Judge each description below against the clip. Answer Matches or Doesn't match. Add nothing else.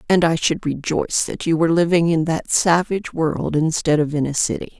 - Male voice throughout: Doesn't match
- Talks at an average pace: Doesn't match